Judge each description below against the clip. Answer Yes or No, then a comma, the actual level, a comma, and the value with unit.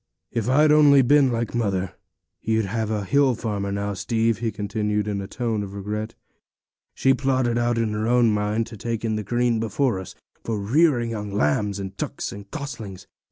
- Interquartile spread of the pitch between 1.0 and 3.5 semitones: Yes, average, 2.9 semitones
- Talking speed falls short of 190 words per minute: No, average, 195 wpm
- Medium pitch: No, low, 110 Hz